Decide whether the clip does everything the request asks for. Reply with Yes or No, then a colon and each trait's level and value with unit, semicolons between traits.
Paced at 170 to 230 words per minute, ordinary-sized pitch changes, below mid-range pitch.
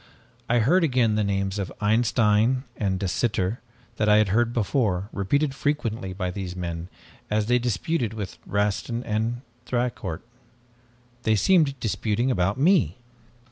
No: average, 140 wpm; average, 3.8 semitones; low, 110 Hz